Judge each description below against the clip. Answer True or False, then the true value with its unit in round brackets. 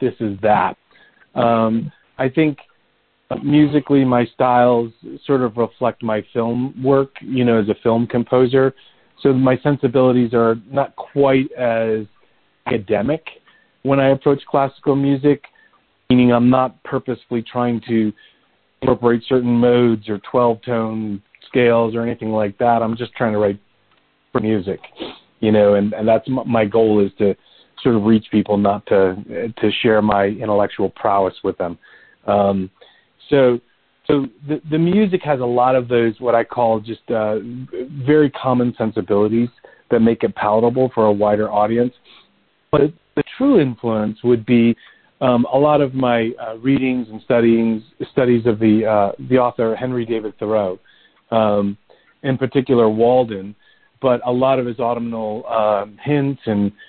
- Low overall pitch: True (120 Hz)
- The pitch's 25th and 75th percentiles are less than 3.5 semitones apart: True (3.1 semitones)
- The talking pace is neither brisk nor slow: True (150 wpm)